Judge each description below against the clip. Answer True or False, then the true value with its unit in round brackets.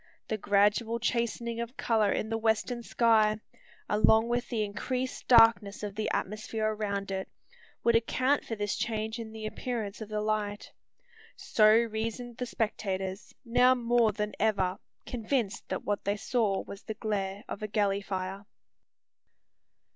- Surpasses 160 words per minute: False (150 wpm)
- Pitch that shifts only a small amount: True (2.2 semitones)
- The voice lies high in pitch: True (215 Hz)